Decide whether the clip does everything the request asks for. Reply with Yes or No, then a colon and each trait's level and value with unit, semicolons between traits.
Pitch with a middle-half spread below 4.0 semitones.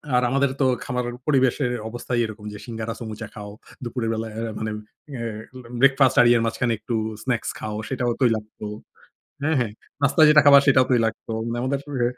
Yes: average, 2.9 semitones